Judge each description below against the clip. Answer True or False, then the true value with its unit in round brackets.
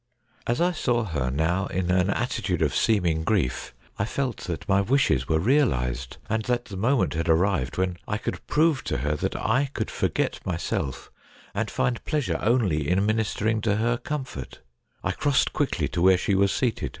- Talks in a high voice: False (100 Hz)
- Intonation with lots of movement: True (6.6 semitones)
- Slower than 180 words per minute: False (185 wpm)